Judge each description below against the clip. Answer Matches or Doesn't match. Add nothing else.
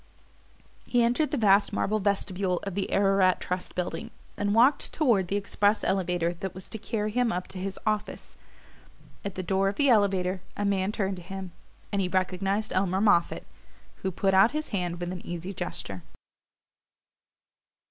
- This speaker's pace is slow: Doesn't match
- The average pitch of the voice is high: Matches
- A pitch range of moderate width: Doesn't match